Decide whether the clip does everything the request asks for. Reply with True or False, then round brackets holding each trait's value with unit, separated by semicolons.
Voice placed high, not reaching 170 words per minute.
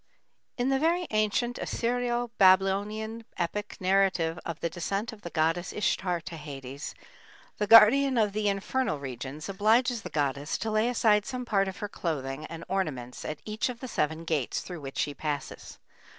False (195 Hz; 175 wpm)